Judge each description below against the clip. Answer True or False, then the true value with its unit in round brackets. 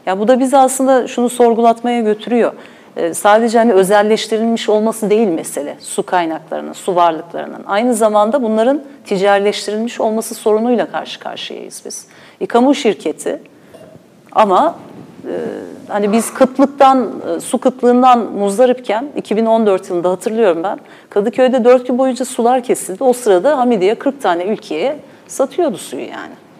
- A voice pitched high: True (230 Hz)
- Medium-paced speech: True (130 wpm)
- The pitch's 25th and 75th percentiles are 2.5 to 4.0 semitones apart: True (3.6 semitones)